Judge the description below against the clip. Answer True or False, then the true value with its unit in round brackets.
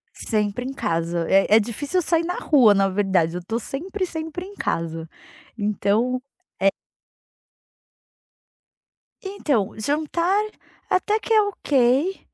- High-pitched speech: True (250 Hz)